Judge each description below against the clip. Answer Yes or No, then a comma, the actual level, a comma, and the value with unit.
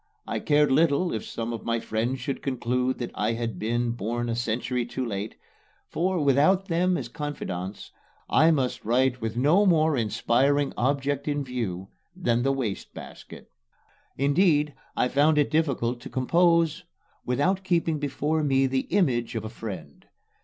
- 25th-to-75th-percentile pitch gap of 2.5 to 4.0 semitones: No, average, 4.4 semitones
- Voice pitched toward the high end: No, low, 135 Hz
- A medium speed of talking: Yes, average, 155 wpm